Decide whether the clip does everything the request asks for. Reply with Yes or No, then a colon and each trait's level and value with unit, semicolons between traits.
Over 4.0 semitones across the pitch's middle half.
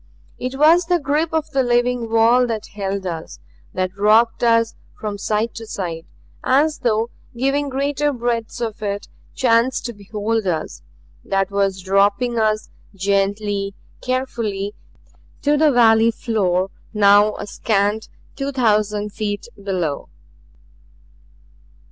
No: average, 3.7 semitones